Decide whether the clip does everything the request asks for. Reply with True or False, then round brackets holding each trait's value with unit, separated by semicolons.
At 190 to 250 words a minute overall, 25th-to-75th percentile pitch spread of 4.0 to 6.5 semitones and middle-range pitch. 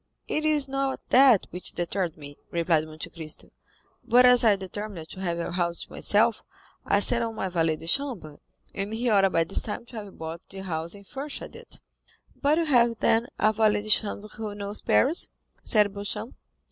False (195 wpm; 5.6 semitones; 205 Hz)